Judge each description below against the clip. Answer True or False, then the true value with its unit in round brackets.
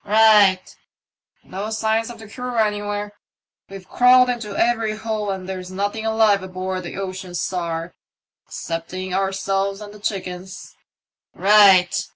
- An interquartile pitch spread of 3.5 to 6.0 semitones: False (2.7 semitones)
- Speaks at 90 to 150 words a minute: True (135 wpm)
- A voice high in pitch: True (200 Hz)